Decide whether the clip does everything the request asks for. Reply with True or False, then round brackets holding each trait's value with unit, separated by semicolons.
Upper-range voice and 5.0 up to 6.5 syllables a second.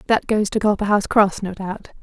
True (205 Hz; 6.0 syllables/s)